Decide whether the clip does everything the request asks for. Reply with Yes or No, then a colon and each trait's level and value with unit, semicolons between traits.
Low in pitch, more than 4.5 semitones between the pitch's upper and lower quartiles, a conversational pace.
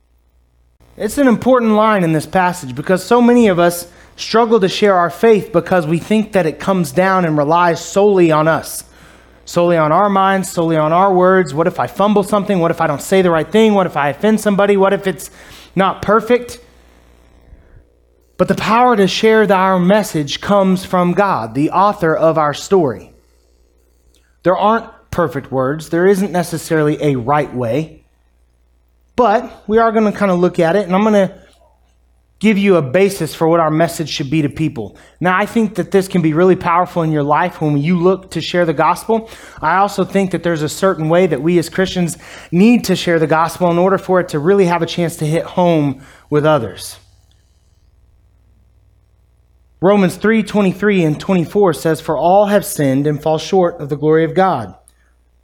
No: medium, 170 Hz; average, 4.9 semitones; average, 195 wpm